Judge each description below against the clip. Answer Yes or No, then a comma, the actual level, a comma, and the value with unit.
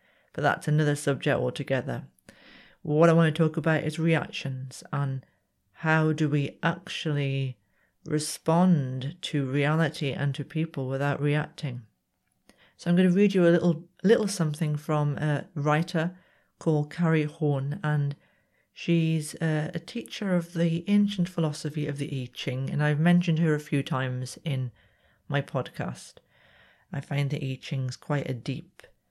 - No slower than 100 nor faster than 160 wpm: Yes, average, 150 wpm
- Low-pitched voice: No, medium, 150 Hz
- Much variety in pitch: No, average, 2.8 semitones